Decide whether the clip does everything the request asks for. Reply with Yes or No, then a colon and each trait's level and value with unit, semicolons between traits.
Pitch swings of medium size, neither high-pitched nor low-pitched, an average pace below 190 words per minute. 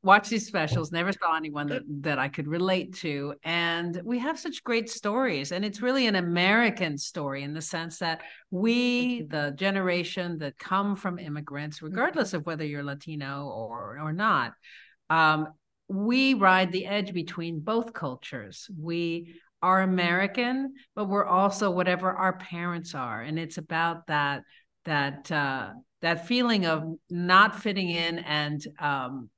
Yes: average, 4.5 semitones; medium, 175 Hz; average, 155 wpm